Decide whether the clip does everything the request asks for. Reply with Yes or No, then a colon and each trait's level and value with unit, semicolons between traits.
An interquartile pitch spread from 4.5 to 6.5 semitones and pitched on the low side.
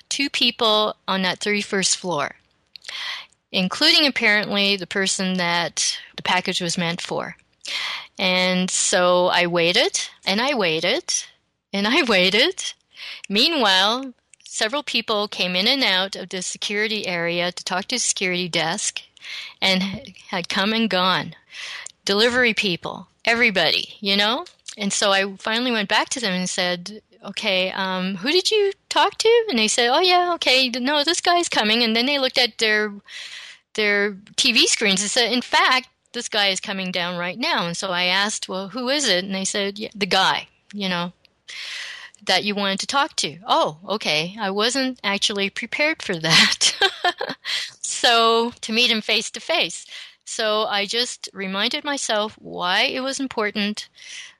No: average, 5.2 semitones; high, 210 Hz